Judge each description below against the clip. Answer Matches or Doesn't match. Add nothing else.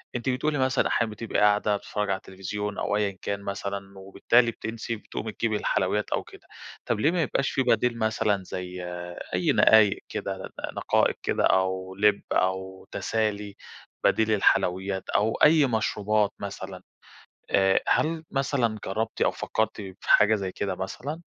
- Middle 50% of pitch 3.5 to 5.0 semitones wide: Doesn't match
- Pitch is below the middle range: Matches